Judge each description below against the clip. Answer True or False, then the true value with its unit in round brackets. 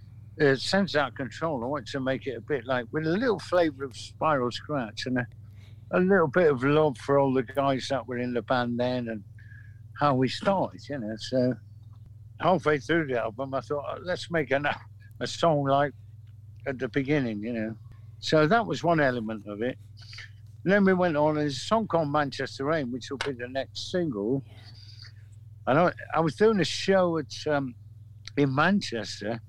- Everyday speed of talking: True (190 wpm)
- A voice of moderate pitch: False (130 Hz)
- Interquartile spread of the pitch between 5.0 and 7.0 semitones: True (5.4 semitones)